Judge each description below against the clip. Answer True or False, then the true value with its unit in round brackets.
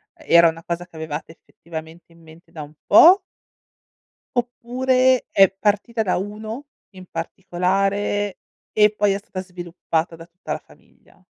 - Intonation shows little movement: False (4.0 semitones)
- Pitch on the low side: False (190 Hz)